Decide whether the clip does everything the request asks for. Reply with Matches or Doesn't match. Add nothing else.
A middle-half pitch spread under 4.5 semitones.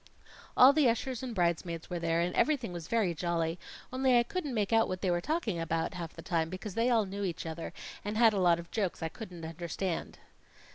Doesn't match